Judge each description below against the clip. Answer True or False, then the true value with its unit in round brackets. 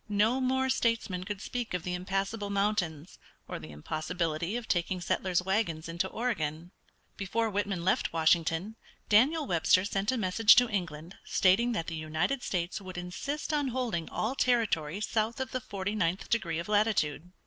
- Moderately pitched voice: False (195 Hz)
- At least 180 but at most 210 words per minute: False (165 wpm)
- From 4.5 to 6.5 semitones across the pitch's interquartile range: True (4.9 semitones)